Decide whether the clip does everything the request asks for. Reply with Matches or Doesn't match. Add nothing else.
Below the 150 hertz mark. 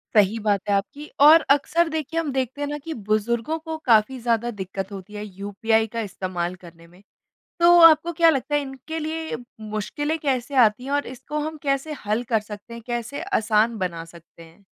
Doesn't match